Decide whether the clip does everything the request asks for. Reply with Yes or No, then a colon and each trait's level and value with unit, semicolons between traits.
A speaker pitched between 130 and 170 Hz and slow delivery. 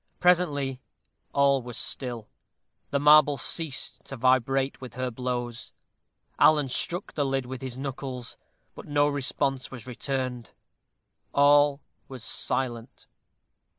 Yes: low, 135 Hz; slow, 115 wpm